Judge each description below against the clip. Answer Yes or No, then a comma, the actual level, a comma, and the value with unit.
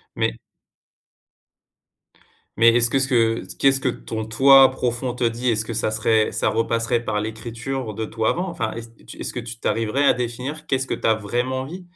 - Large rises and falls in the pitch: No, average, 2.8 semitones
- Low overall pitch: Yes, low, 120 Hz